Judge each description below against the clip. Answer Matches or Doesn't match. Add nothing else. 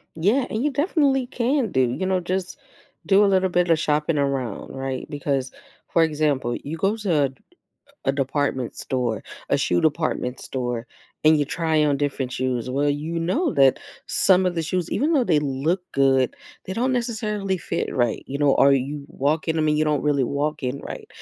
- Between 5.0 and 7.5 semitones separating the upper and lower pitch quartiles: Matches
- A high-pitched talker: Doesn't match